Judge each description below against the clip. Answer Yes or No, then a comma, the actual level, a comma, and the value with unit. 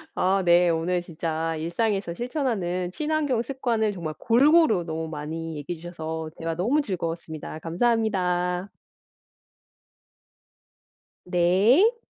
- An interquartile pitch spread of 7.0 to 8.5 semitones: No, wide, 5.6 semitones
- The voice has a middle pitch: Yes, medium, 180 Hz